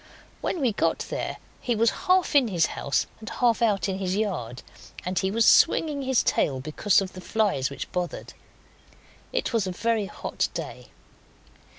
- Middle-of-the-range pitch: No, high, 205 Hz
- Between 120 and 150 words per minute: No, average, 175 wpm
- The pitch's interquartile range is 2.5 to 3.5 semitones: No, average, 4.3 semitones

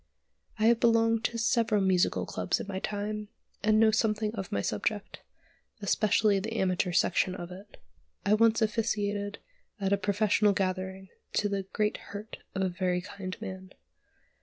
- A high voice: Yes, high, 205 Hz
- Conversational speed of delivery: Yes, average, 160 wpm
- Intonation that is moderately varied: No, narrow, 2.2 semitones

